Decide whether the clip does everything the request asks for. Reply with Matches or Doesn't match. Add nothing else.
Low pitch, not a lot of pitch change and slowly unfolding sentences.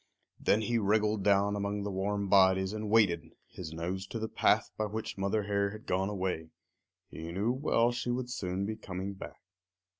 Doesn't match